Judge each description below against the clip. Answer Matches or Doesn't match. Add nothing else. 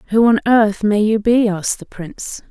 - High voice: Matches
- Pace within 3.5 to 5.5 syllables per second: Matches